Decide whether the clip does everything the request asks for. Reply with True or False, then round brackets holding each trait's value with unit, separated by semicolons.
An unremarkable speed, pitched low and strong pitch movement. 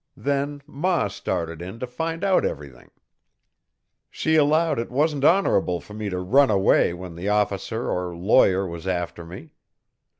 True (155 wpm; 105 Hz; 8.1 semitones)